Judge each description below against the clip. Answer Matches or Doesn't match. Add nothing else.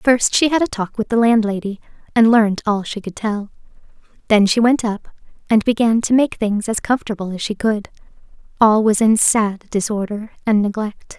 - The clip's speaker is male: Doesn't match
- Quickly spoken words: Doesn't match